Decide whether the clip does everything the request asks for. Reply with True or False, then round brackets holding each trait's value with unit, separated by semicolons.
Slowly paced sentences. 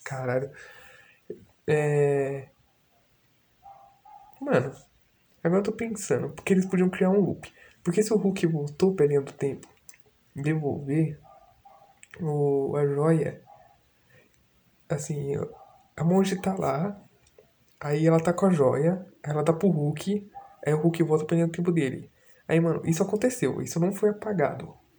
False (130 wpm)